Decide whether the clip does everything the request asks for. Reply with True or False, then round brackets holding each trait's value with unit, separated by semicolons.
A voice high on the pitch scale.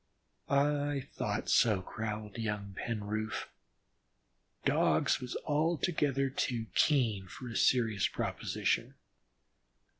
False (115 Hz)